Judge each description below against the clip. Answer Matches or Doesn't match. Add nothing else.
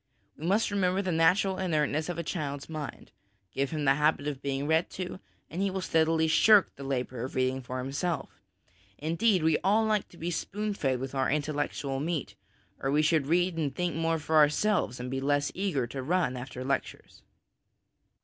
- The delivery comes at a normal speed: Matches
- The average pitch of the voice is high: Doesn't match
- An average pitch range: Matches